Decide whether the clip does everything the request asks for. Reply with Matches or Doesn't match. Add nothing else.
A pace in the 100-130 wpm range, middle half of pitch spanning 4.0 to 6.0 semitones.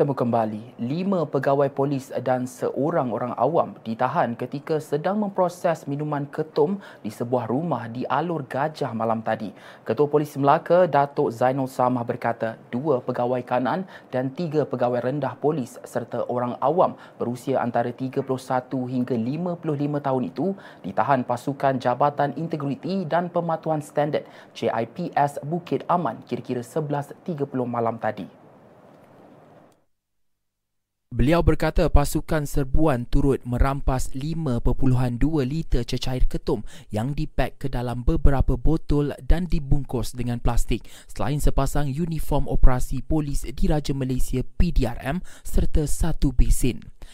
Doesn't match